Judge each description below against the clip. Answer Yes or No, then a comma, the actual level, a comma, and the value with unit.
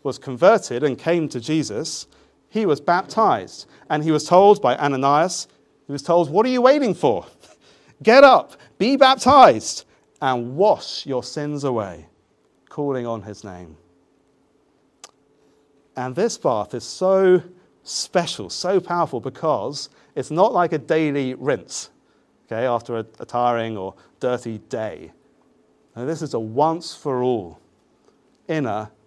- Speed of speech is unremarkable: No, slow, 130 wpm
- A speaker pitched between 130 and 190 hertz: Yes, medium, 140 Hz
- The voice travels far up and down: Yes, wide, 6.3 semitones